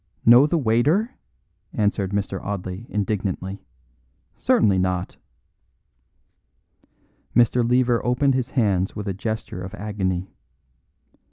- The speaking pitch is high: No, low, 105 Hz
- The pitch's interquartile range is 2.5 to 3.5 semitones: No, average, 4.2 semitones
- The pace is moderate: No, slow, 100 wpm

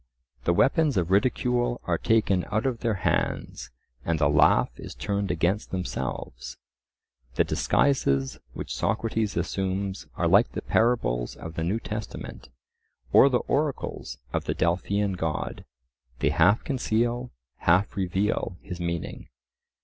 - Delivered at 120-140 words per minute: Yes, slow, 135 wpm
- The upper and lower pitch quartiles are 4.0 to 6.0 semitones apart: Yes, average, 5.2 semitones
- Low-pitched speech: Yes, very low, 95 Hz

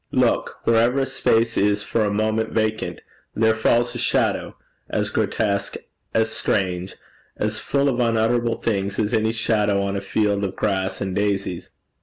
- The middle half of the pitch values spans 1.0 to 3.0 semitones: Yes, narrow, 2.4 semitones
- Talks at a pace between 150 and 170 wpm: Yes, average, 160 wpm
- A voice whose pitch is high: No, low, 110 Hz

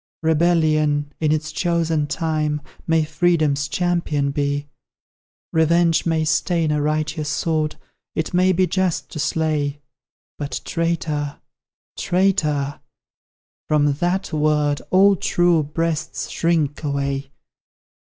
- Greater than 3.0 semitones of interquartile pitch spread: No, narrow, 2.4 semitones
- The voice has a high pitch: No, medium, 155 Hz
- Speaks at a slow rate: Yes, slow, 105 wpm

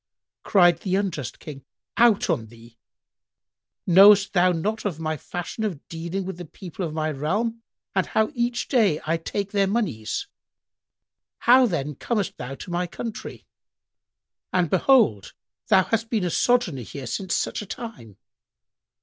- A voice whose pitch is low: No, medium, 180 Hz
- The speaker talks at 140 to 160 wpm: Yes, average, 150 wpm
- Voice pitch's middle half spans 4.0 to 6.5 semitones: Yes, wide, 5.5 semitones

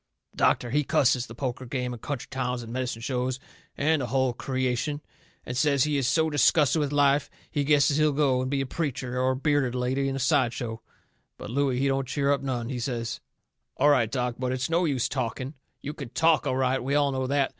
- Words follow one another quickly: Yes, fast, 225 wpm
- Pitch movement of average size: No, narrow, 2.3 semitones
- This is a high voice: No, low, 130 Hz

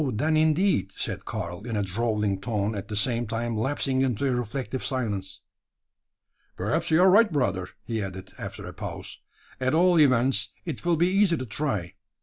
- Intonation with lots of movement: Yes, wide, 6.6 semitones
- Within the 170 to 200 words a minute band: Yes, average, 175 wpm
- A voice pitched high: No, low, 120 Hz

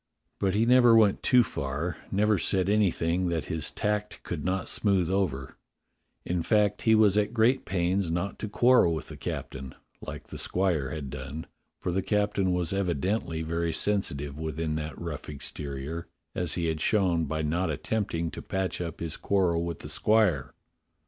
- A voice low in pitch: Yes, very low, 90 Hz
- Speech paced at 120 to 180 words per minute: Yes, average, 170 wpm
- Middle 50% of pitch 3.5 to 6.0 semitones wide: Yes, average, 4.2 semitones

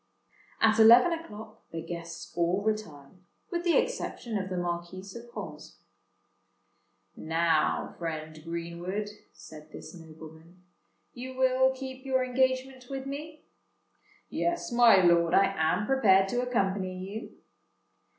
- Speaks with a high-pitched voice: Yes, high, 200 Hz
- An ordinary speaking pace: No, slow, 120 wpm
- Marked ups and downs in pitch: Yes, wide, 7.1 semitones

